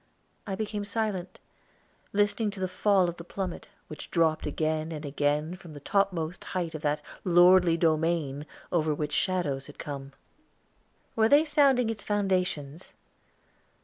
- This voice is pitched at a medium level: Yes, medium, 175 Hz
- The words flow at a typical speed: Yes, average, 145 wpm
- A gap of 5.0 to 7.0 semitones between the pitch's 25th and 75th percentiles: No, average, 4.5 semitones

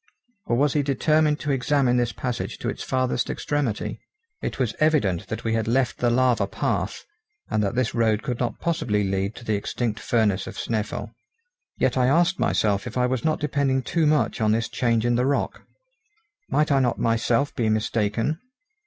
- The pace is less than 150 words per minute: No, average, 190 wpm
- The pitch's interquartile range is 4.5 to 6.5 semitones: No, average, 3.9 semitones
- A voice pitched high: No, low, 125 Hz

